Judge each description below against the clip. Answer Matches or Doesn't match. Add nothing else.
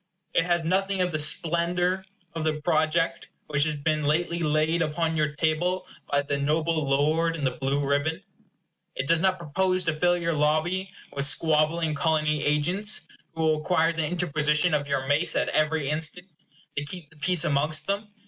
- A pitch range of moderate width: Doesn't match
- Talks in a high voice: Doesn't match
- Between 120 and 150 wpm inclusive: Doesn't match